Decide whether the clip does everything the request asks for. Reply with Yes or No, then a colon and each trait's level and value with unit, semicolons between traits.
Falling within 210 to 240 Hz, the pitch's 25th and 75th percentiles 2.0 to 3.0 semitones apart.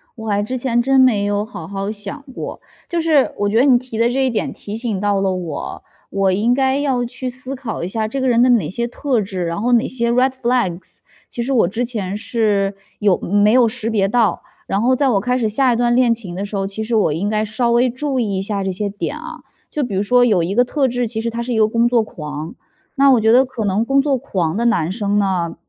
No: high, 225 Hz; average, 3.7 semitones